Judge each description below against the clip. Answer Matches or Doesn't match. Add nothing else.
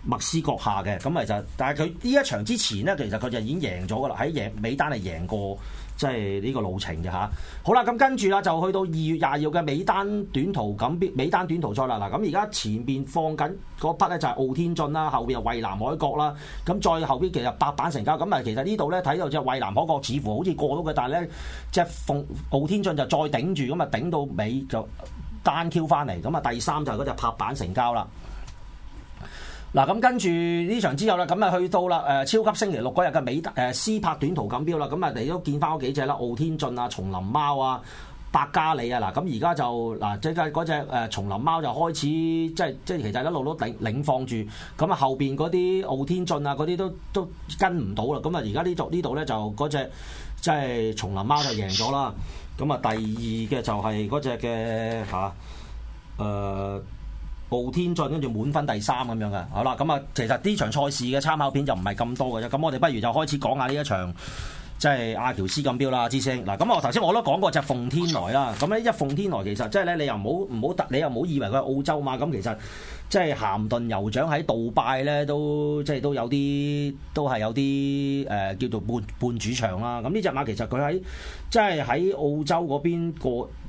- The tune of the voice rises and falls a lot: Matches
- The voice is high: Doesn't match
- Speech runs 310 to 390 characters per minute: Matches